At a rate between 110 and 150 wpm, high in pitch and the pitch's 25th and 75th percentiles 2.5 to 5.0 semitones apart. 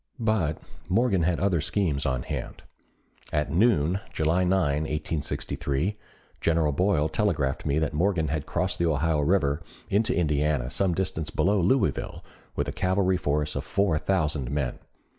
No: average, 145 wpm; very low, 80 Hz; average, 4.1 semitones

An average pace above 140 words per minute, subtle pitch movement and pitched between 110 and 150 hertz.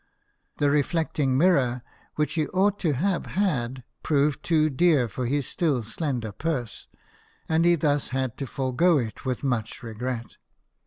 No: average, 150 wpm; average, 4.4 semitones; medium, 140 Hz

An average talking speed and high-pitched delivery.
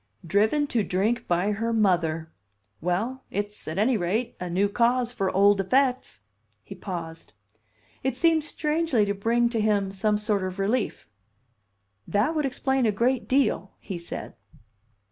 Yes: average, 150 wpm; high, 210 Hz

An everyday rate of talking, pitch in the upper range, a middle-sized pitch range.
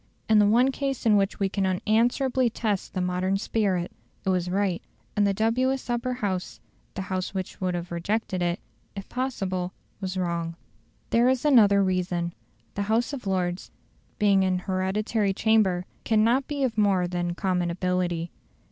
Yes: average, 165 wpm; high, 195 Hz; average, 3.5 semitones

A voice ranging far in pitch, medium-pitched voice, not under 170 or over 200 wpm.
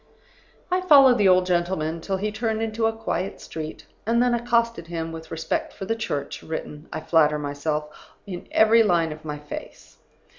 Yes: wide, 6.1 semitones; medium, 180 Hz; average, 180 wpm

